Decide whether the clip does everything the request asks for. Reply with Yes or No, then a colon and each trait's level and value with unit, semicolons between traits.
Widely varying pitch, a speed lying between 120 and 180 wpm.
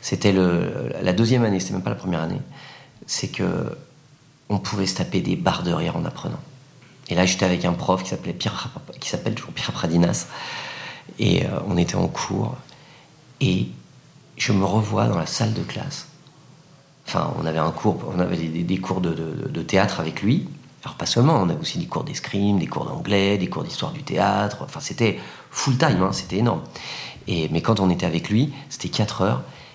No: wide, 7.4 semitones; average, 200 wpm